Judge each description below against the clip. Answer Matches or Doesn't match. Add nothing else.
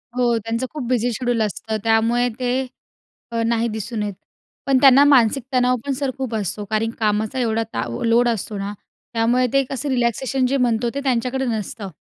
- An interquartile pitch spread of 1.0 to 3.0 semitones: Matches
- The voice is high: Matches